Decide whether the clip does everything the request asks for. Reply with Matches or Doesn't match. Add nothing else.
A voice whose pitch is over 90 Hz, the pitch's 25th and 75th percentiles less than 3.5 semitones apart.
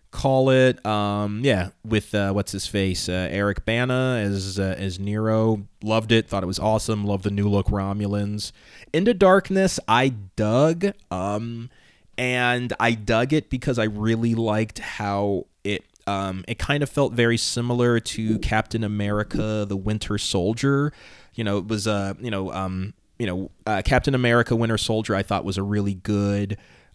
Matches